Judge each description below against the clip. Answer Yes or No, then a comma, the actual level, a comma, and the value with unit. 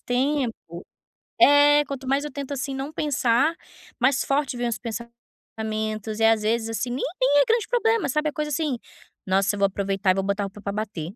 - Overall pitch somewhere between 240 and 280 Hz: Yes, high, 245 Hz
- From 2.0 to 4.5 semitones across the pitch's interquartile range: No, average, 4.9 semitones